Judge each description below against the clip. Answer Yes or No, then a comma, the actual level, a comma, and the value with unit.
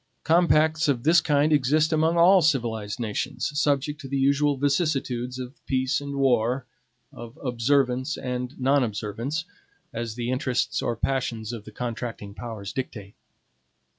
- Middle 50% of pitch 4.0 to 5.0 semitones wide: No, average, 3.5 semitones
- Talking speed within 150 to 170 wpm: No, average, 140 wpm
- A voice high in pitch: No, low, 130 Hz